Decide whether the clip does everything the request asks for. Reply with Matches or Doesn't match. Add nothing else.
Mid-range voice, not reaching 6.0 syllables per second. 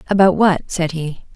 Matches